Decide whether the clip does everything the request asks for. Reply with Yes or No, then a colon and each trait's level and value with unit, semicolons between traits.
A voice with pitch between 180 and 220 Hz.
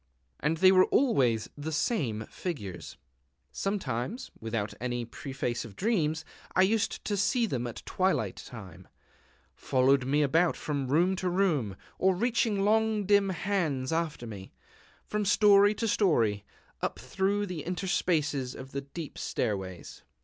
No: medium, 160 Hz